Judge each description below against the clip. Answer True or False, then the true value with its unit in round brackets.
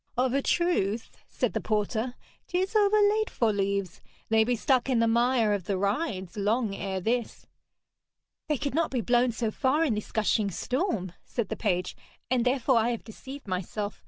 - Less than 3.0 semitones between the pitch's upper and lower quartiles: False (4.4 semitones)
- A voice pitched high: True (230 Hz)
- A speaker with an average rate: True (180 wpm)